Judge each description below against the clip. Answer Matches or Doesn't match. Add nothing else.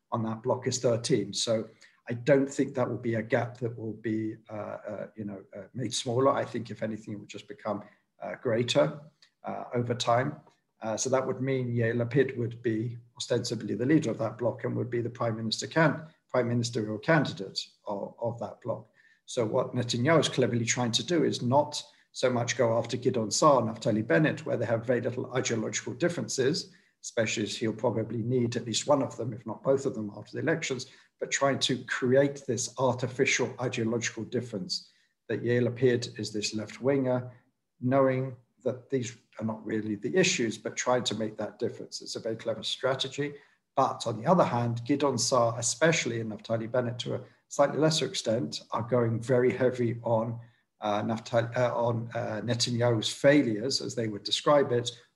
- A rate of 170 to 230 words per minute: Matches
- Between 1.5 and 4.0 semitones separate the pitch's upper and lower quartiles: Matches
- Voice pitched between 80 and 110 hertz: Doesn't match